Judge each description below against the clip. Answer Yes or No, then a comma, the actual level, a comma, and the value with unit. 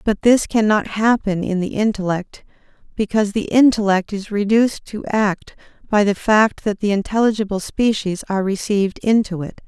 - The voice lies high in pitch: Yes, high, 205 Hz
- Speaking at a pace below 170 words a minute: Yes, average, 155 wpm